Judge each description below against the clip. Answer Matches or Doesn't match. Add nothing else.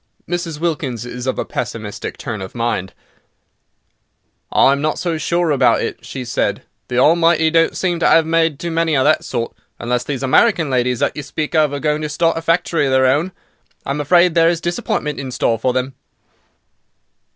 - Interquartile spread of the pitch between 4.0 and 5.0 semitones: Matches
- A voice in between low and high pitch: Matches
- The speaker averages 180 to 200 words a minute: Matches